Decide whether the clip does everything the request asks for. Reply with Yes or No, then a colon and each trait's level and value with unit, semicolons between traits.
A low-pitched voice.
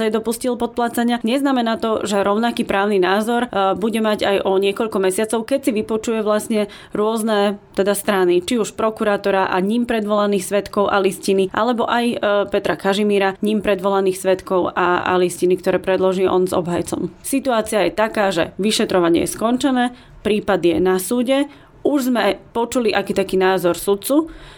No: high, 205 Hz